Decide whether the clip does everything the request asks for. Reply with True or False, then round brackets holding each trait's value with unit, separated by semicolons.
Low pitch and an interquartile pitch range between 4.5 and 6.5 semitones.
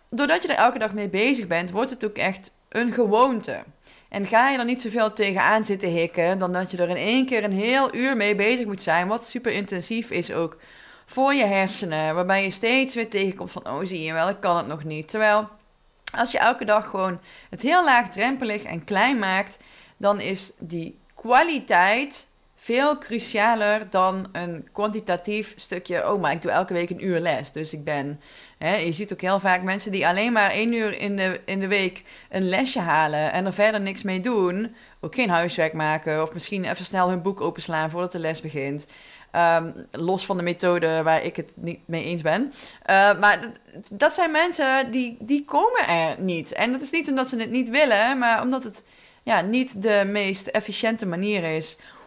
False (200 Hz; 4.8 semitones)